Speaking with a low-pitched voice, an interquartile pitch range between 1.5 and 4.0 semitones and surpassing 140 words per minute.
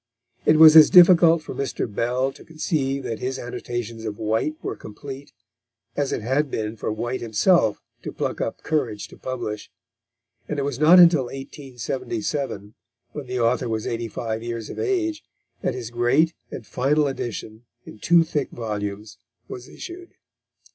No: low, 130 Hz; average, 5.0 semitones; average, 160 wpm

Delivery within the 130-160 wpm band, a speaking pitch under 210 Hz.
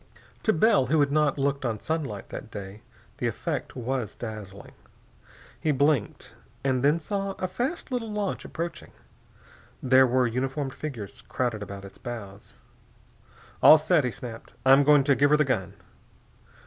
Yes: average, 155 wpm; low, 135 Hz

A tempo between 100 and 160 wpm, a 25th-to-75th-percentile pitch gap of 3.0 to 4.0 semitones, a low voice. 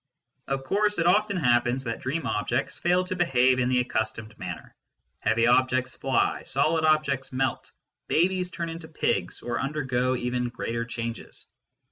No: average, 150 wpm; average, 5.0 semitones; low, 130 Hz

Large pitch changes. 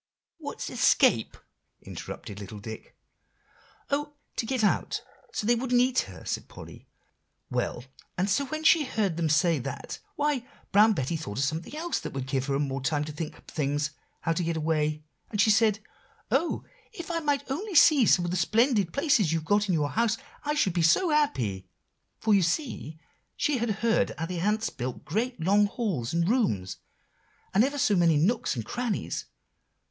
Yes: wide, 8.5 semitones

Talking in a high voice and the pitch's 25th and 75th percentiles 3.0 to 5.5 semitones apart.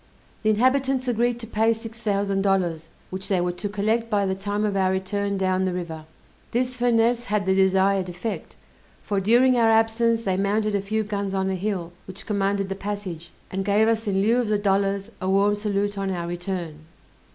No: high, 200 Hz; narrow, 2.6 semitones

